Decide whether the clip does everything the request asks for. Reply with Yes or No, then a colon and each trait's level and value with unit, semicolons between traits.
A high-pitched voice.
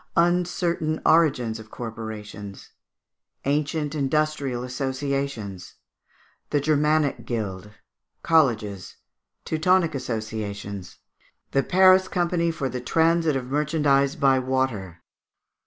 No: low, 135 Hz